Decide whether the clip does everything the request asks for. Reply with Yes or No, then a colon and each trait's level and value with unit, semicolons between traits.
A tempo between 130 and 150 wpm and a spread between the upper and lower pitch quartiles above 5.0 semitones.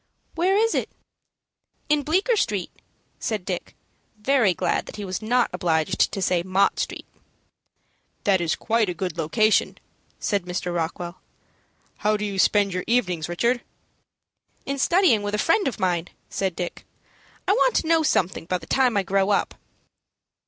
No: average, 160 wpm; wide, 5.6 semitones